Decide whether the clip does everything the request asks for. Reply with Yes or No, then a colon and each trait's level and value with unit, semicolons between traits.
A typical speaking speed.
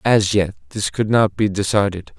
Yes: average, 190 wpm